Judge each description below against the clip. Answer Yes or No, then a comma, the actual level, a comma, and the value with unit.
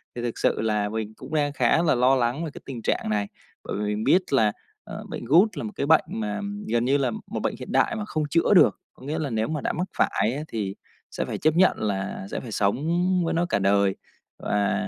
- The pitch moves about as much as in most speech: No, wide, 6.7 semitones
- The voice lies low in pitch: Yes, low, 125 Hz